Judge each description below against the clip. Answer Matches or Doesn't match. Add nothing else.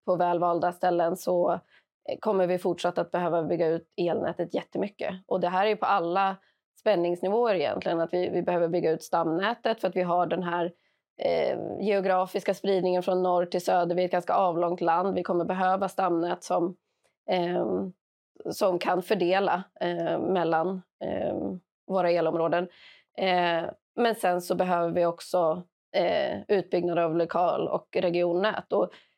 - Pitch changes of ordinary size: Doesn't match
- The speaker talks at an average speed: Matches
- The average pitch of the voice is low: Doesn't match